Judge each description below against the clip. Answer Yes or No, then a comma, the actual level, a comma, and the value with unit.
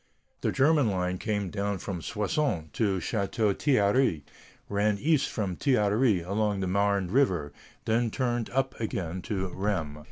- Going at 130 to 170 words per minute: Yes, average, 150 wpm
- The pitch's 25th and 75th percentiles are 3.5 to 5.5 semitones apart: Yes, average, 4.0 semitones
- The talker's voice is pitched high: No, low, 100 Hz